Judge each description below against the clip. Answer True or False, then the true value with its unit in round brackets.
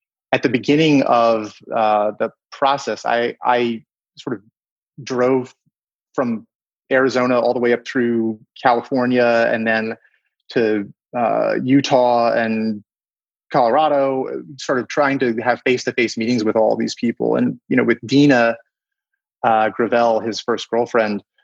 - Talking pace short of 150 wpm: True (140 wpm)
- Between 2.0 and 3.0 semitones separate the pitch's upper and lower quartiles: True (2.6 semitones)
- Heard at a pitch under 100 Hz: False (120 Hz)